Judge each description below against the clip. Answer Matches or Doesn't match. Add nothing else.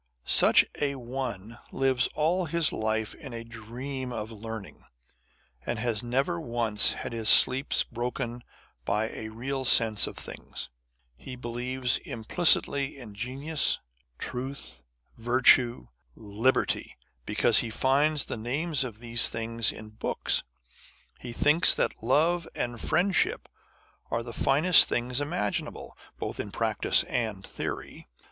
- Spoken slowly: Matches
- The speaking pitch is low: Matches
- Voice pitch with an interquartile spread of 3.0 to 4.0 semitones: Matches